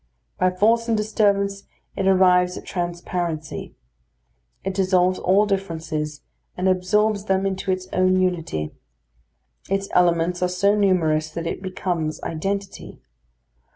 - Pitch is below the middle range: No, medium, 185 Hz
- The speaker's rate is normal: No, slow, 120 wpm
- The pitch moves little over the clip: Yes, narrow, 2.2 semitones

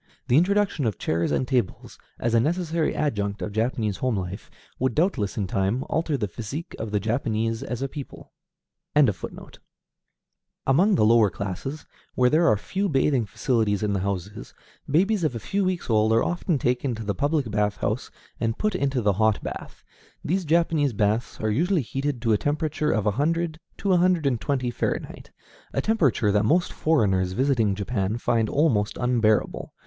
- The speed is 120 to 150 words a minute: No, average, 175 wpm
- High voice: No, low, 125 Hz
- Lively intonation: Yes, wide, 6.4 semitones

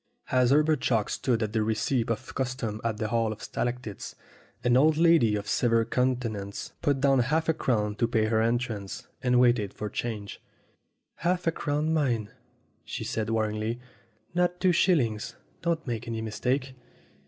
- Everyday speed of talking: Yes, average, 165 wpm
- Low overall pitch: Yes, low, 120 Hz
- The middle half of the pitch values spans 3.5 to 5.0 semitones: Yes, average, 3.9 semitones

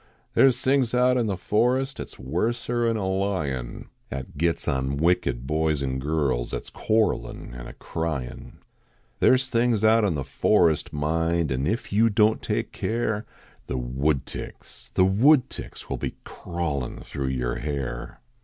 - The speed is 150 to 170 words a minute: Yes, average, 165 wpm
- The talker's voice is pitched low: Yes, very low, 85 Hz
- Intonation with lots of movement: Yes, wide, 8.7 semitones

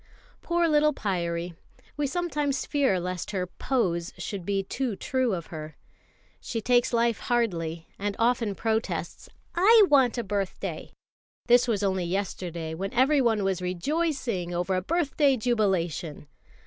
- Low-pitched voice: No, high, 210 Hz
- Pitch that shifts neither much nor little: No, wide, 6.4 semitones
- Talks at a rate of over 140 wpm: No, slow, 135 wpm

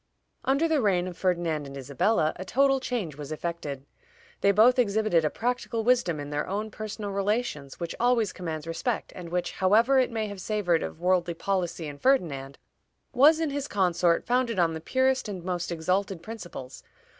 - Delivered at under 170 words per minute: No, average, 180 wpm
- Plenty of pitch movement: Yes, wide, 5.8 semitones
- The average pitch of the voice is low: No, high, 190 Hz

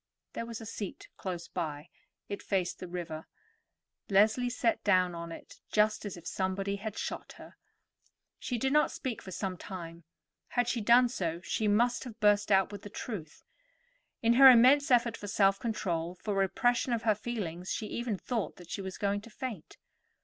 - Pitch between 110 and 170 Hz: No, high, 205 Hz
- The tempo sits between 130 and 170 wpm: No, average, 185 wpm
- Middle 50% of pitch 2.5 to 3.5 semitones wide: No, average, 4.1 semitones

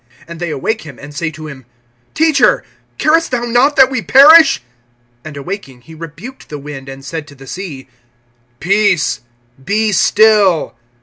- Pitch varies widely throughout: Yes, wide, 7.2 semitones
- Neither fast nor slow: Yes, average, 160 wpm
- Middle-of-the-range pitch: Yes, medium, 175 Hz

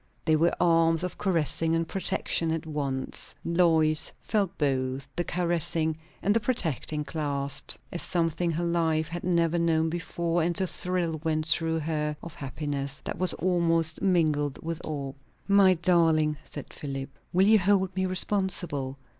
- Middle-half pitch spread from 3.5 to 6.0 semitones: No, narrow, 2.5 semitones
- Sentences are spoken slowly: No, average, 155 wpm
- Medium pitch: Yes, medium, 165 Hz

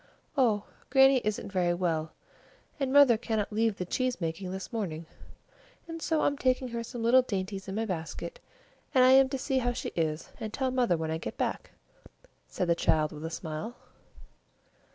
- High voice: Yes, high, 220 Hz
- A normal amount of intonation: No, wide, 6.7 semitones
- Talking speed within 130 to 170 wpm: No, average, 185 wpm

